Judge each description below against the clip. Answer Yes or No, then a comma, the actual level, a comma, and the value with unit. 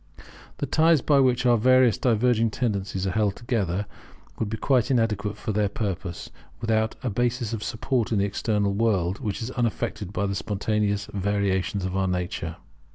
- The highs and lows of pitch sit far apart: No, average, 3.2 semitones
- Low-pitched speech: Yes, low, 105 Hz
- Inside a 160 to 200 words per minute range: Yes, average, 170 wpm